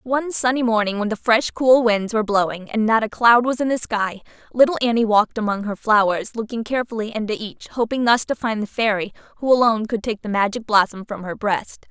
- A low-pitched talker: No, high, 225 Hz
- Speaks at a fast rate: Yes, fast, 220 wpm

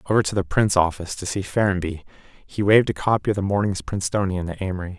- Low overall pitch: Yes, very low, 95 Hz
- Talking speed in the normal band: No, fast, 215 wpm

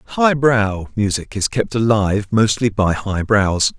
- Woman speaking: No, male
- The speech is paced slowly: Yes, slow, 125 wpm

